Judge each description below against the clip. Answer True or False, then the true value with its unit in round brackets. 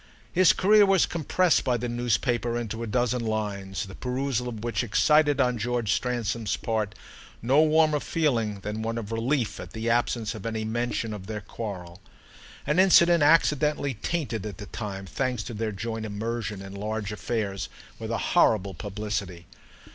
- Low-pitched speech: True (115 Hz)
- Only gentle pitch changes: False (3.3 semitones)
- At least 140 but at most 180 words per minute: True (165 wpm)